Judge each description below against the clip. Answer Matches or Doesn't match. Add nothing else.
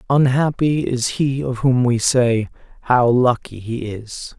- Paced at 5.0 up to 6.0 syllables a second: Doesn't match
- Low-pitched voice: Matches